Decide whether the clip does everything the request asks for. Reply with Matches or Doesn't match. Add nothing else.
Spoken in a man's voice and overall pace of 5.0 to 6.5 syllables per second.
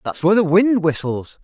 Matches